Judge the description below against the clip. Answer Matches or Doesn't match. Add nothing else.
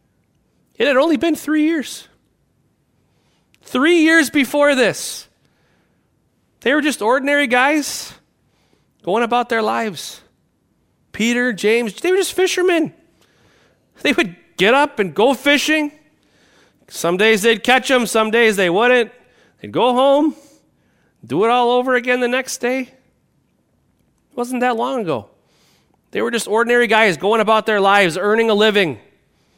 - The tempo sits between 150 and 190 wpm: Doesn't match